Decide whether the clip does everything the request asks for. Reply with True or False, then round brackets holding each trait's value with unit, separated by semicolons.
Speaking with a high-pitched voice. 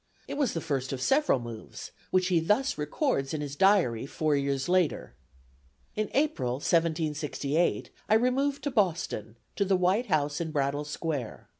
False (160 Hz)